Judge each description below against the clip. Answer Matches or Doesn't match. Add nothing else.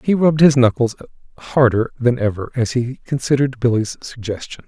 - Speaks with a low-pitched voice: Matches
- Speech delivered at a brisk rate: Doesn't match